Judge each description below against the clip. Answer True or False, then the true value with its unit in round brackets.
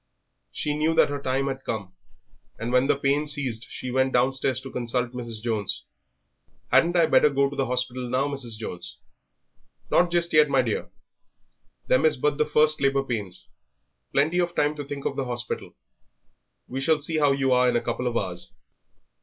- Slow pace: False (185 wpm)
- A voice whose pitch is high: False (135 Hz)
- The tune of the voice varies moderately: True (3.1 semitones)